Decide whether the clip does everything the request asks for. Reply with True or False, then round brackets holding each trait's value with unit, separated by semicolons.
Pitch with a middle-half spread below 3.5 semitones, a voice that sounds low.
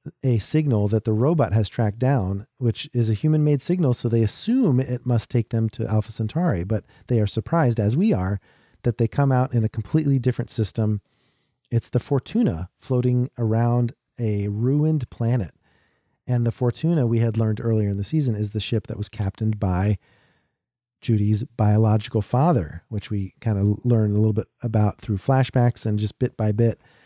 True (2.9 semitones; 115 Hz)